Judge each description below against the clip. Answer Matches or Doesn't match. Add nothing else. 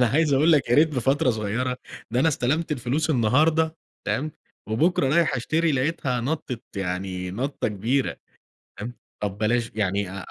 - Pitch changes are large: Matches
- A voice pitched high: Doesn't match